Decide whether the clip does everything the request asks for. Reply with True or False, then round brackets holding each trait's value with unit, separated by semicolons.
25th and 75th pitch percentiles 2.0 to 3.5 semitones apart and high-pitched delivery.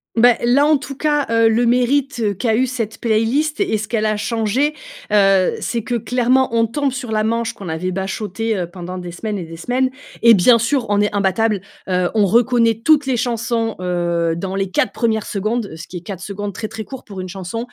False (4.0 semitones; 220 Hz)